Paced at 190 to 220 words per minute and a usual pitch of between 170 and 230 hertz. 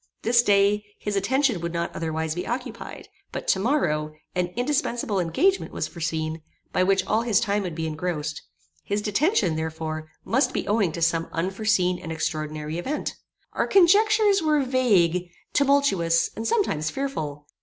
No: average, 155 wpm; high, 190 Hz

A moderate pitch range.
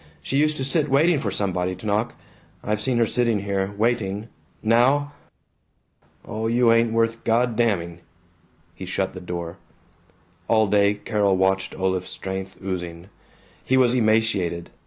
Yes: average, 3.7 semitones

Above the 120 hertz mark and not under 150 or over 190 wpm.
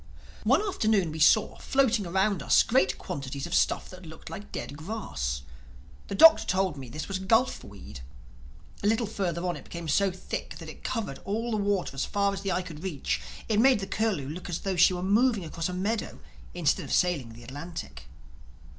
No: medium, 185 Hz; average, 200 wpm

